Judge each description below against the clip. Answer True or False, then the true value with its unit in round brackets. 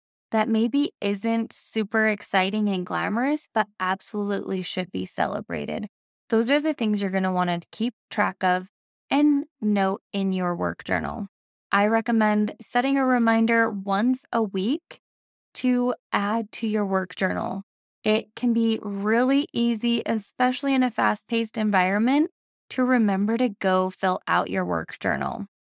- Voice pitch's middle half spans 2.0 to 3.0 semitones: False (3.4 semitones)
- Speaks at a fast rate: False (150 wpm)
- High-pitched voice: True (220 Hz)